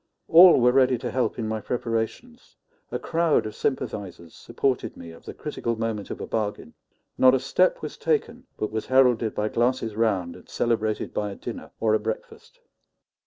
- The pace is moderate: Yes, average, 180 wpm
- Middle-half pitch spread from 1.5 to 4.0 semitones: Yes, average, 3.3 semitones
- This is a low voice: Yes, low, 115 Hz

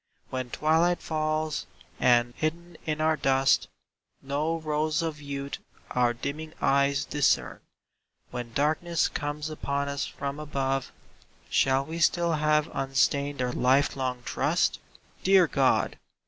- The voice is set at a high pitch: No, medium, 145 Hz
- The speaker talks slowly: Yes, slow, 125 wpm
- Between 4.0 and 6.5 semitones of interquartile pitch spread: No, narrow, 2.5 semitones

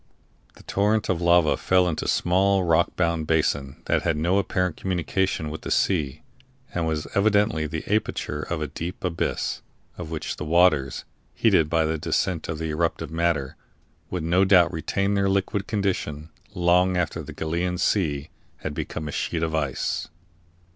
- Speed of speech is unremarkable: Yes, average, 170 wpm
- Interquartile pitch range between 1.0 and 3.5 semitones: Yes, average, 2.9 semitones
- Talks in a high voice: No, very low, 85 Hz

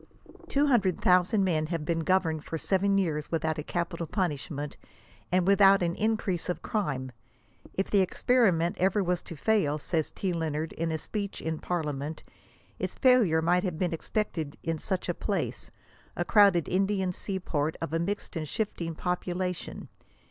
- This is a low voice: No, medium, 175 Hz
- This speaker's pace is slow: No, average, 185 wpm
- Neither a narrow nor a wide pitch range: Yes, average, 3.4 semitones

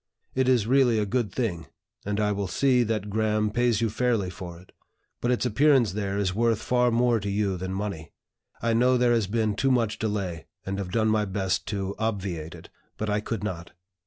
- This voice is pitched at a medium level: No, low, 105 Hz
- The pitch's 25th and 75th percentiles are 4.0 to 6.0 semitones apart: No, average, 3.3 semitones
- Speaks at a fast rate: Yes, fast, 210 wpm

